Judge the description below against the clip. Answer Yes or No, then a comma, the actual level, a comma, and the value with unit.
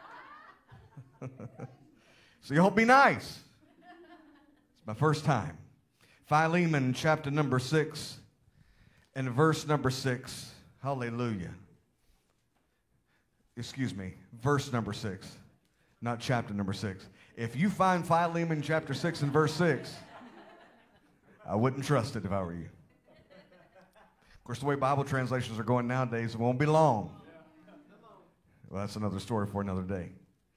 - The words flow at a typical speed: No, slow, 125 wpm